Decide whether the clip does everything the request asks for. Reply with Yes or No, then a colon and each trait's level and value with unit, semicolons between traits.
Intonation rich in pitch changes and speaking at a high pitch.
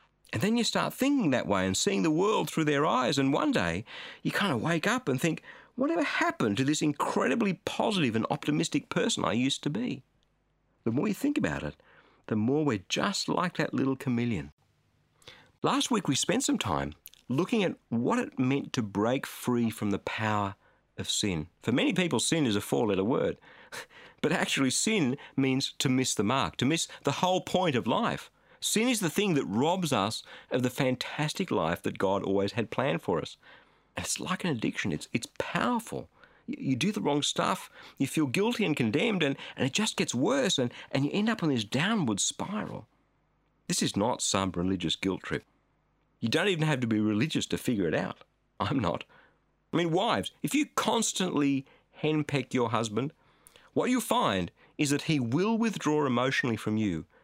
No: wide, 8.9 semitones; medium, 145 Hz